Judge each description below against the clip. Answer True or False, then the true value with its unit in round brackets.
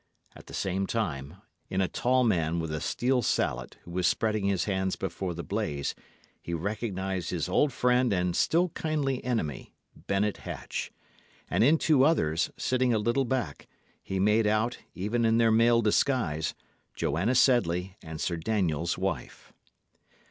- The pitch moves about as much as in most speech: False (5.7 semitones)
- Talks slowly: False (155 wpm)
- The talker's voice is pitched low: True (100 Hz)